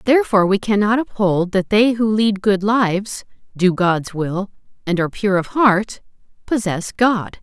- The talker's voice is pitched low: No, high, 205 Hz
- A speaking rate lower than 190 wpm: Yes, average, 160 wpm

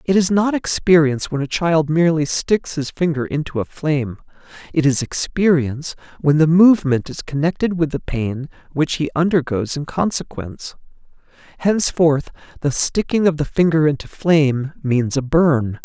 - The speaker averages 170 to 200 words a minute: No, average, 155 wpm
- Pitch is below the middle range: No, medium, 155 Hz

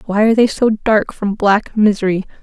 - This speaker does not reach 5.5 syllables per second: Yes, 5.1 syllables/s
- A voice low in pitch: No, high, 210 Hz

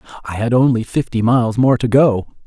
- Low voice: Yes, low, 120 Hz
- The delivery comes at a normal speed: Yes, average, 195 wpm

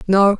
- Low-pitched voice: No, high, 195 Hz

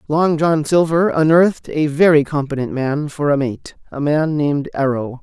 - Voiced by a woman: No, male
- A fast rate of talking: No, average, 170 wpm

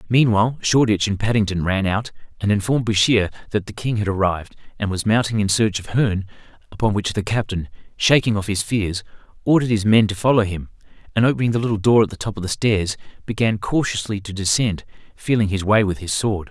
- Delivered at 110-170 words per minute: No, fast, 205 wpm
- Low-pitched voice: Yes, low, 105 Hz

